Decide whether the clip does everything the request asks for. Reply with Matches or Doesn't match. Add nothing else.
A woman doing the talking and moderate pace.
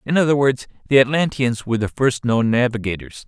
Doesn't match